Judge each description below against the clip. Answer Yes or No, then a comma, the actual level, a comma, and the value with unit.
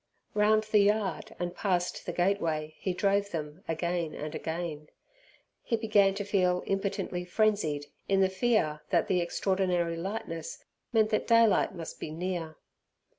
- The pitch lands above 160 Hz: Yes, medium, 185 Hz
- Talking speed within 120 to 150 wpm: Yes, average, 145 wpm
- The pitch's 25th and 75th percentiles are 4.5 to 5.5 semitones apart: No, average, 3.6 semitones